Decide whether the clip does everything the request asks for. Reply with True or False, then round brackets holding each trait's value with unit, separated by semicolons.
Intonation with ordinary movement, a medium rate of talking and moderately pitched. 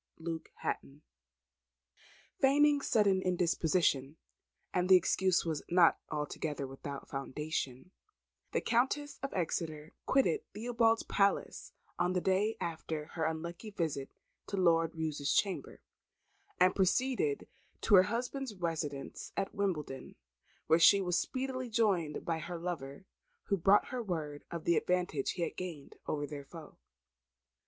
False (4.4 semitones; 130 wpm; 175 Hz)